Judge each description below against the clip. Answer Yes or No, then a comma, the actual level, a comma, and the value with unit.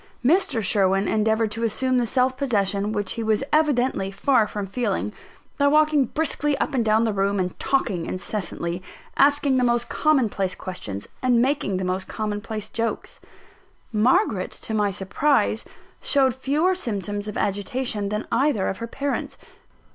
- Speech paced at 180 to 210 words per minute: No, average, 160 wpm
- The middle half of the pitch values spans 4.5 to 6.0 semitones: Yes, average, 4.8 semitones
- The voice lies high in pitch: Yes, high, 220 Hz